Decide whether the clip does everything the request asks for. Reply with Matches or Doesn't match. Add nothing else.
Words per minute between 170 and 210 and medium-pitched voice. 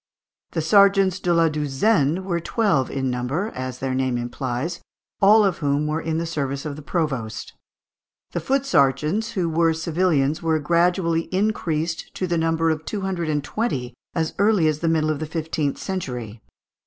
Matches